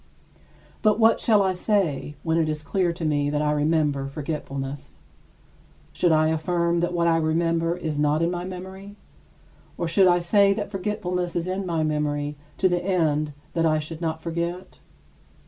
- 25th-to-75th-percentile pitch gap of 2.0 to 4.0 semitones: Yes, average, 3.0 semitones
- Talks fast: No, average, 175 wpm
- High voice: No, medium, 165 Hz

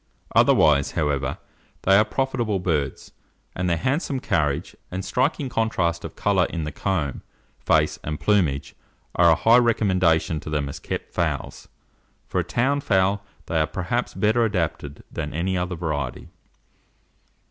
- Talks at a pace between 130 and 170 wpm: Yes, average, 145 wpm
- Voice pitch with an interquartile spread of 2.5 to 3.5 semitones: No, wide, 5.6 semitones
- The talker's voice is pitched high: No, very low, 90 Hz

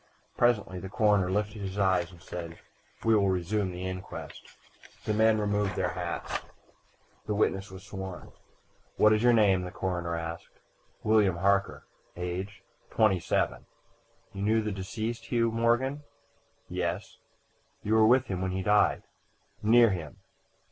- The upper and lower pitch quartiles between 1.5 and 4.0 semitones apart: Yes, average, 2.7 semitones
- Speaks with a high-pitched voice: No, low, 100 Hz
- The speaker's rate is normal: Yes, average, 145 wpm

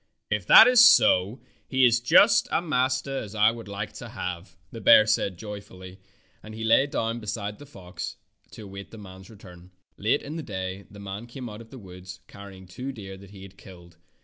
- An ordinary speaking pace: No, fast, 210 wpm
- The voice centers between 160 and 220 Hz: No, low, 105 Hz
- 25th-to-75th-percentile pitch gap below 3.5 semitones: No, average, 3.8 semitones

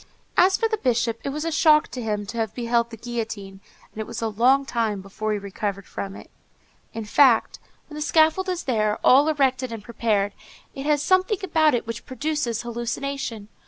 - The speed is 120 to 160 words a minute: No, average, 195 wpm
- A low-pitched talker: No, high, 240 Hz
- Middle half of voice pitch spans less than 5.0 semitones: No, wide, 5.4 semitones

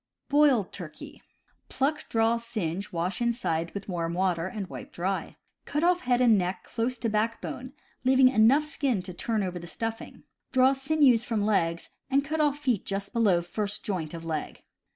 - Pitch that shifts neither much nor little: No, wide, 5.9 semitones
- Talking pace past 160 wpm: Yes, average, 175 wpm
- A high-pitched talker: Yes, high, 225 Hz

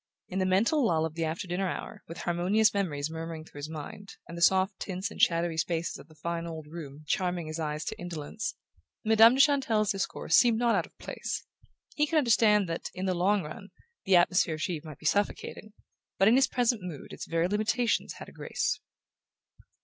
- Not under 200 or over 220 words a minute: Yes, fast, 205 wpm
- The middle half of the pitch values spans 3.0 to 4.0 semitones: No, average, 4.5 semitones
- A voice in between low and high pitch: Yes, medium, 180 Hz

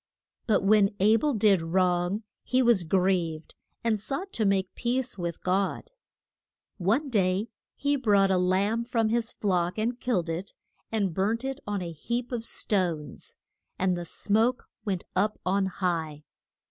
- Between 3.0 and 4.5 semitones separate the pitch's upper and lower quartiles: Yes, average, 4.0 semitones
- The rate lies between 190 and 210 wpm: No, average, 155 wpm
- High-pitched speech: Yes, high, 200 Hz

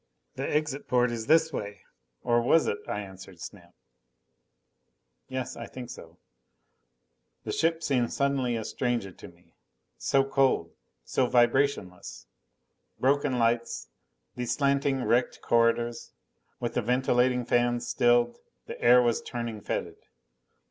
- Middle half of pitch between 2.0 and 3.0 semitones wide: Yes, narrow, 2.5 semitones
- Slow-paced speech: Yes, slow, 130 wpm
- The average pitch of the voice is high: No, low, 120 Hz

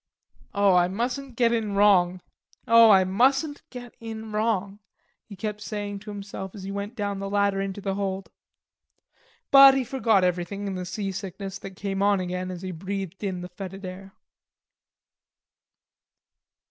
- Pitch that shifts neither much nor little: No, narrow, 2.3 semitones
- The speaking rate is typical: Yes, average, 160 wpm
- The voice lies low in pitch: No, high, 200 Hz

